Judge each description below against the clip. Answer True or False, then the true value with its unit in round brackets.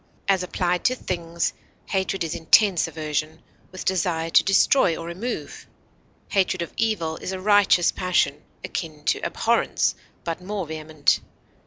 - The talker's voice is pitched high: False (175 Hz)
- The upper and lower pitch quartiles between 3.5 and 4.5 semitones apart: False (2.9 semitones)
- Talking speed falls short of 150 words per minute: True (140 wpm)